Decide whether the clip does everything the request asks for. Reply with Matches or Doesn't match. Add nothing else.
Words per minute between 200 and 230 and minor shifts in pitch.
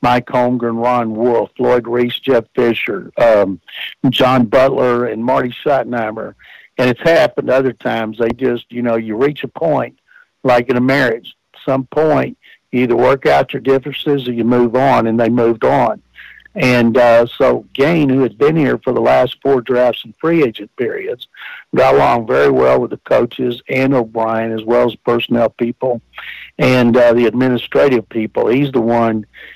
Doesn't match